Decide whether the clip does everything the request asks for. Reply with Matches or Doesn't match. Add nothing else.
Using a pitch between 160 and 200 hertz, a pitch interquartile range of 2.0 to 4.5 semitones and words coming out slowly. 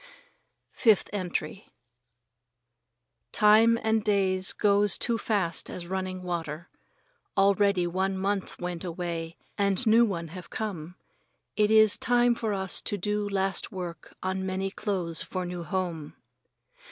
Matches